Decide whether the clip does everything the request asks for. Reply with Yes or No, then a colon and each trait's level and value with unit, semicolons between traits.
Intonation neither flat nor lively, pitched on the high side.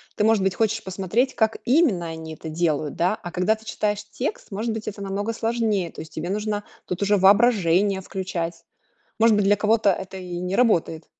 Yes: average, 3.5 semitones; high, 200 Hz